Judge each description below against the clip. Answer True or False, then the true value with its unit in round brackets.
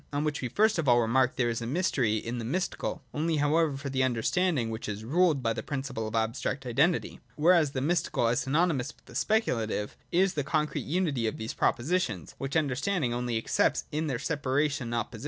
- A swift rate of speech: True (210 wpm)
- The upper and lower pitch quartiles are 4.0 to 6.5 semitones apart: True (5.2 semitones)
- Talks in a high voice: False (135 Hz)